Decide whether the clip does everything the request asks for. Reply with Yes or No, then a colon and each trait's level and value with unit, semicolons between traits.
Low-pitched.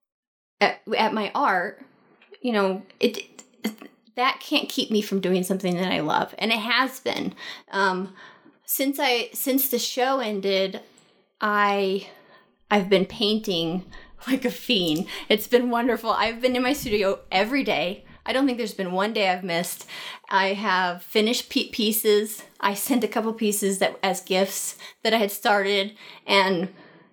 No: high, 210 Hz